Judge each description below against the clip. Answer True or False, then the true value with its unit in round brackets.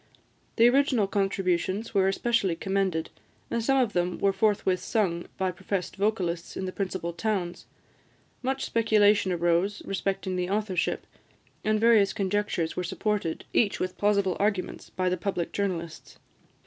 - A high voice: True (195 Hz)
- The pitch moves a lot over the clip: False (2.6 semitones)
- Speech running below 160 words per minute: True (140 wpm)